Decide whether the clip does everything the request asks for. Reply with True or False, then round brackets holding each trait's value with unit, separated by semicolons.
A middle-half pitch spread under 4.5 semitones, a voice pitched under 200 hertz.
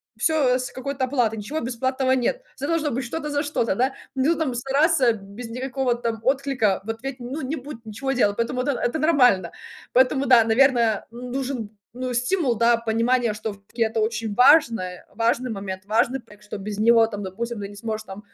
False (3.4 semitones; 240 Hz)